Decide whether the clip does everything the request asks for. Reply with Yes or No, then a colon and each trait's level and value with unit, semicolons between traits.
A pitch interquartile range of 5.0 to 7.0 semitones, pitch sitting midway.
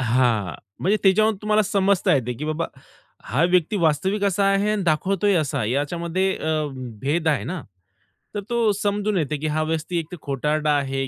Yes: average, 5.3 semitones; medium, 165 Hz